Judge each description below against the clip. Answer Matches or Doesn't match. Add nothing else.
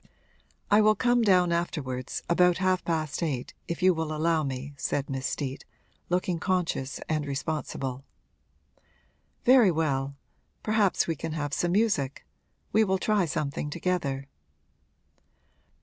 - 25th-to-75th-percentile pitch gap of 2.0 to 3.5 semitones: Doesn't match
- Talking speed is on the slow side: Matches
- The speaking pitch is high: Doesn't match